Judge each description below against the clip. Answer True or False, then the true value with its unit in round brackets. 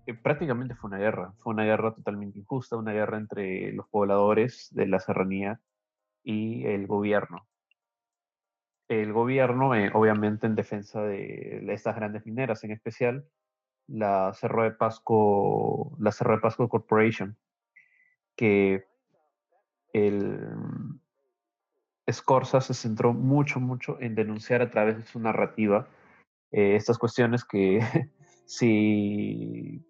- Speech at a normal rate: False (120 wpm)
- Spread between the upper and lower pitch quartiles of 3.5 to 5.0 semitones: False (2.8 semitones)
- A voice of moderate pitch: False (110 Hz)